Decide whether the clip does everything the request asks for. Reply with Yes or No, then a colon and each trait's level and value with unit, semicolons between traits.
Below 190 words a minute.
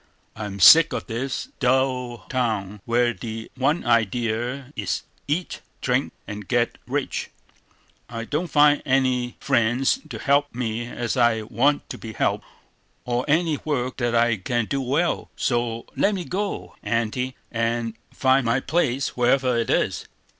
Yes: average, 145 wpm